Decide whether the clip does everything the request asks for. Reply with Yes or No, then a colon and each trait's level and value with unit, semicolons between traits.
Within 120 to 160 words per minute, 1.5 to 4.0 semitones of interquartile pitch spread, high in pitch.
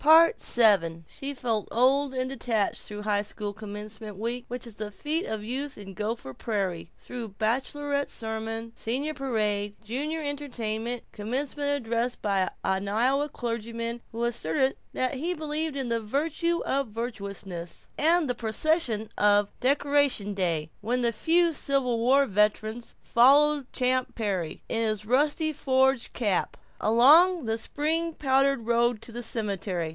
No: average, 140 wpm; average, 4.7 semitones; high, 235 Hz